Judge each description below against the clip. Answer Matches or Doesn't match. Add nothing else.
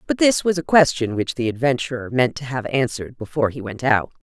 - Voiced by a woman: Matches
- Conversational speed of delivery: Doesn't match